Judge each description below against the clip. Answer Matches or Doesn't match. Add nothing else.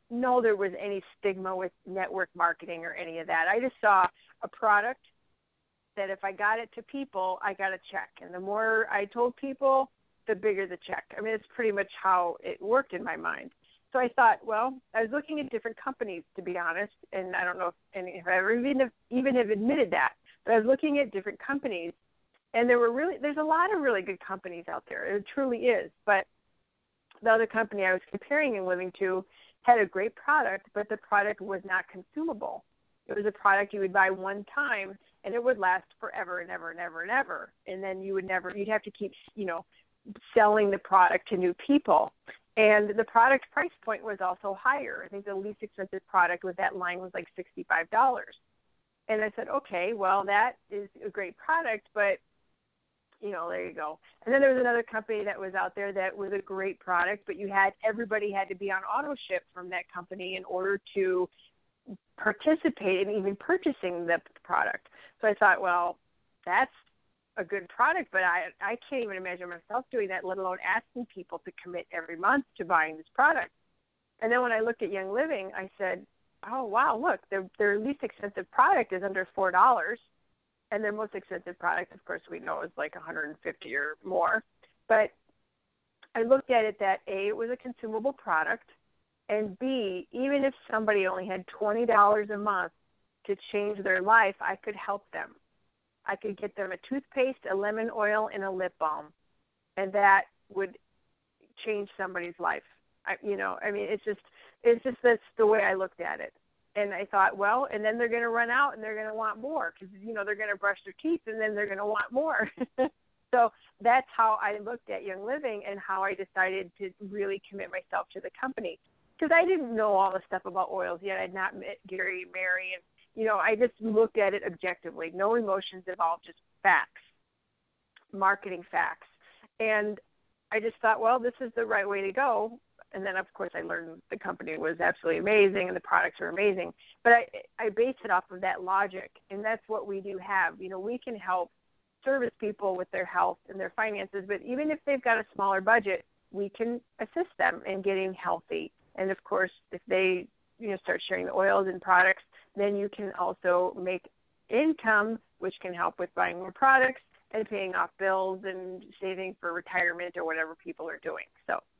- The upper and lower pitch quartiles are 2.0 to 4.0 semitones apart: Matches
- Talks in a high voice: Matches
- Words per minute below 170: Doesn't match